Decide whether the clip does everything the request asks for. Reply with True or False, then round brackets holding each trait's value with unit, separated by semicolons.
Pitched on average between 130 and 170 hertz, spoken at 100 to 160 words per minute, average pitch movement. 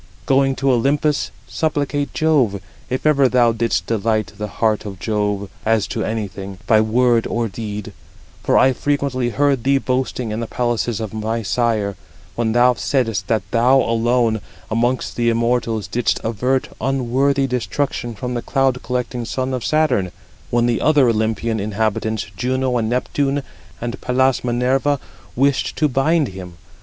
False (120 Hz; 150 wpm; 3.1 semitones)